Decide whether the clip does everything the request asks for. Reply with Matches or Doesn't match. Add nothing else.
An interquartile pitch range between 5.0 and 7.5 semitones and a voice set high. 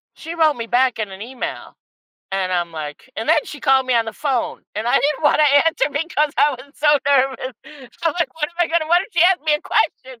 Doesn't match